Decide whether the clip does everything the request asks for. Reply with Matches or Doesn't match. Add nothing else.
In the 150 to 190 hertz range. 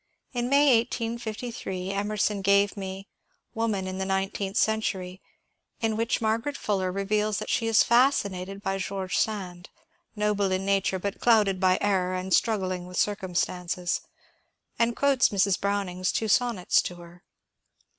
Doesn't match